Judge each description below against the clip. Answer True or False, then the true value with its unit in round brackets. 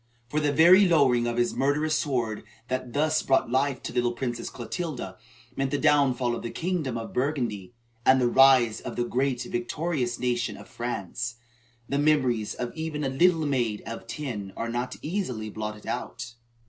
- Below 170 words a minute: False (180 wpm)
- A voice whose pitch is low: True (130 Hz)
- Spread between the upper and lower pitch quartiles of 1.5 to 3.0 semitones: False (3.7 semitones)